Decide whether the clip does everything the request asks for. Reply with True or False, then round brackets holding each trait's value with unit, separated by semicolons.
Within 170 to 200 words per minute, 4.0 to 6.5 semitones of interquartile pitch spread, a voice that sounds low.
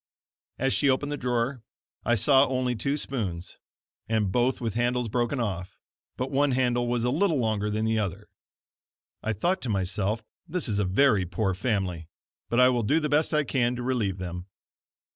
True (185 wpm; 4.3 semitones; 120 Hz)